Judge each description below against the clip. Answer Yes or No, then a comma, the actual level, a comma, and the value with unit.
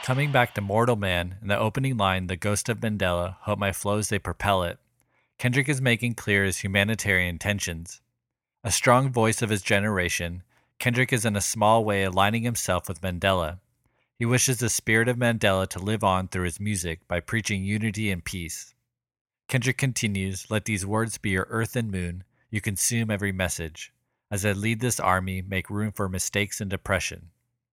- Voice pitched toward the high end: No, low, 105 Hz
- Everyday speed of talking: Yes, average, 180 wpm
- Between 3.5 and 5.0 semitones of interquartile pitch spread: Yes, average, 3.8 semitones